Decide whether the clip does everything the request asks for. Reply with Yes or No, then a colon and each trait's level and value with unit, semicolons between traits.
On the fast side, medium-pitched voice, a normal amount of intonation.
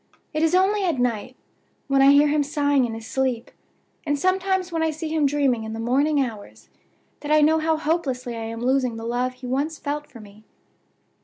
No: fast, 210 wpm; very high, 280 Hz; average, 4.2 semitones